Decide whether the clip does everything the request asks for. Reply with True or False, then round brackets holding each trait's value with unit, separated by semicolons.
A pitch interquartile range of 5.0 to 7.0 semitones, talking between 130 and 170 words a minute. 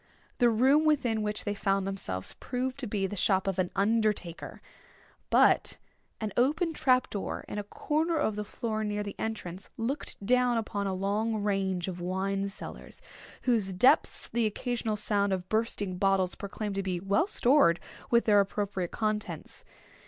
False (3.2 semitones; 165 wpm)